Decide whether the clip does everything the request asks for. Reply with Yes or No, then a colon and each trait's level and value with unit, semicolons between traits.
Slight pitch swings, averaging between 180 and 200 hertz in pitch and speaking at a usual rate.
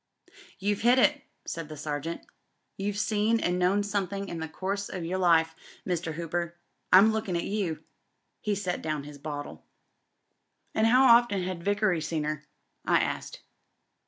No: average, 4.0 semitones; medium, 185 Hz; average, 160 wpm